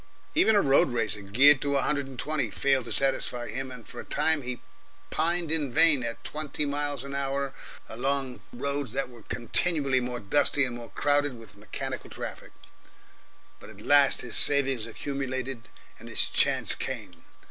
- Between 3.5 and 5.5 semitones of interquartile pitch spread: No, average, 2.8 semitones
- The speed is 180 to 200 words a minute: No, average, 170 wpm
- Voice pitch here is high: No, low, 135 Hz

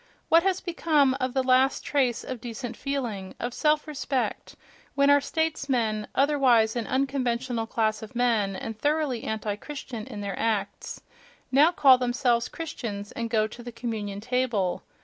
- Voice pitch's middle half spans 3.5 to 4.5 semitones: Yes, average, 4.0 semitones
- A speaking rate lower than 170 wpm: Yes, average, 155 wpm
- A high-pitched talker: Yes, high, 245 Hz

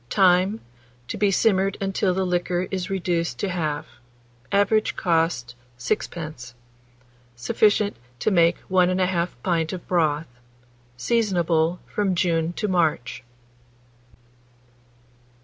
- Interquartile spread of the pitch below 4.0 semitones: Yes, average, 2.9 semitones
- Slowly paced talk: Yes, slow, 105 wpm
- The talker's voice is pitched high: No, medium, 180 Hz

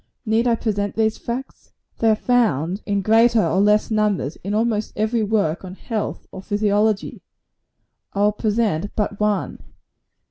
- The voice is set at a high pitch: Yes, high, 210 Hz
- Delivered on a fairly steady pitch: Yes, narrow, 1.7 semitones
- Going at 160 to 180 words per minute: No, average, 150 wpm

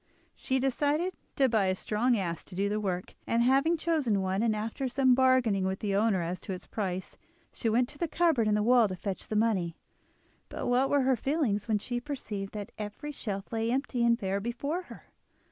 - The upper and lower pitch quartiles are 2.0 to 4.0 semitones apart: No, average, 4.8 semitones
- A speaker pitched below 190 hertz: No, high, 225 Hz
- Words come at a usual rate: No, fast, 215 wpm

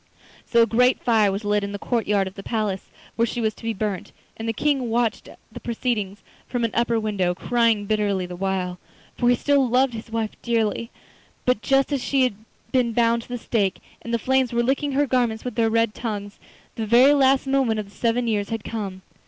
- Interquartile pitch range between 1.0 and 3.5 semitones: Yes, average, 2.9 semitones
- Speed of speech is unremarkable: No, fast, 220 wpm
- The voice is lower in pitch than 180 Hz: No, high, 230 Hz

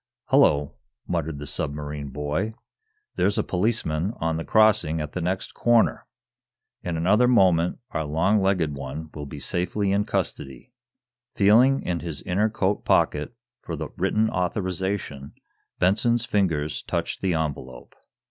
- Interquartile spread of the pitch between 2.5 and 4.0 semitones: No, average, 5.2 semitones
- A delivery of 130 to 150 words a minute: Yes, average, 140 wpm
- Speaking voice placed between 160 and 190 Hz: No, very low, 90 Hz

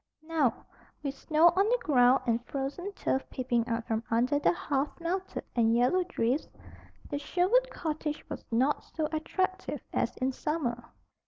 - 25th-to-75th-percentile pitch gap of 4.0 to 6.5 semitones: Yes, wide, 5.5 semitones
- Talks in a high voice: Yes, very high, 290 Hz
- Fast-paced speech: No, average, 155 wpm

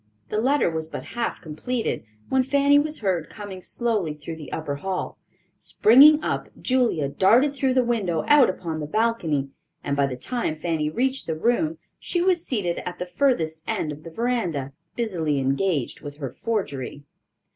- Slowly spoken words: No, average, 170 wpm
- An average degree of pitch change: No, wide, 8.3 semitones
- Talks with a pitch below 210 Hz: Yes, high, 190 Hz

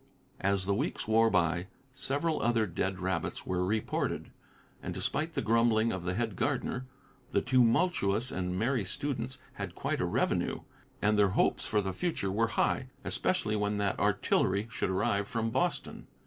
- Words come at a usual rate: Yes, average, 160 wpm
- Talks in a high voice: No, low, 110 Hz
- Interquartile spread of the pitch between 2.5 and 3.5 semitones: No, average, 3.9 semitones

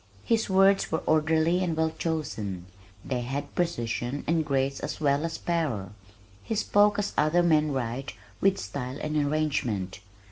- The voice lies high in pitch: No, medium, 155 Hz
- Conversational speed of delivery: Yes, average, 150 wpm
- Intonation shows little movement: No, average, 4.3 semitones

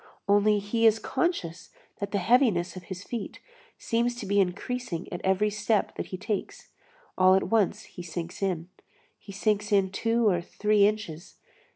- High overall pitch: Yes, high, 200 Hz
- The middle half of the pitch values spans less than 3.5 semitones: Yes, average, 2.8 semitones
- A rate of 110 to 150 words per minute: No, average, 170 wpm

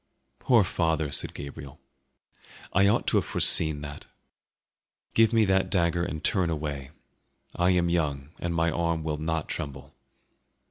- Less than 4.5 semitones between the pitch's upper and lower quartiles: Yes, average, 2.9 semitones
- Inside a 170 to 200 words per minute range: No, average, 145 wpm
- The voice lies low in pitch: Yes, very low, 80 Hz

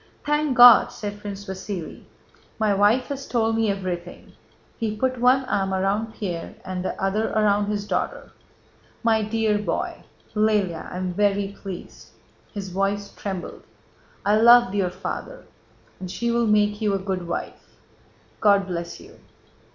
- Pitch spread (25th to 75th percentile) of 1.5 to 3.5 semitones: Yes, average, 2.7 semitones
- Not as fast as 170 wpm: Yes, average, 145 wpm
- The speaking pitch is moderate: No, high, 205 Hz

